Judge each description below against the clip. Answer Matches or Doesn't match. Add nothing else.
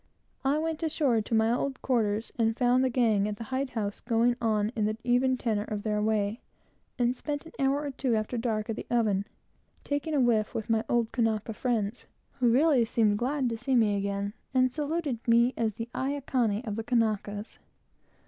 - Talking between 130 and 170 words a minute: Doesn't match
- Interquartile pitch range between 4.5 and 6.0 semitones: Doesn't match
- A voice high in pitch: Matches